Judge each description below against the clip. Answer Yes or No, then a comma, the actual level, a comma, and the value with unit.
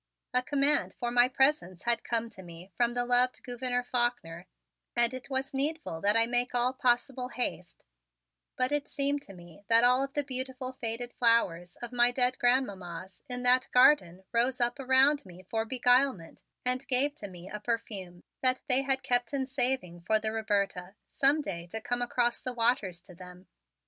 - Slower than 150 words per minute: No, average, 185 wpm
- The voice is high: Yes, high, 245 Hz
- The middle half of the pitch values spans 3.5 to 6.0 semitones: Yes, average, 4.1 semitones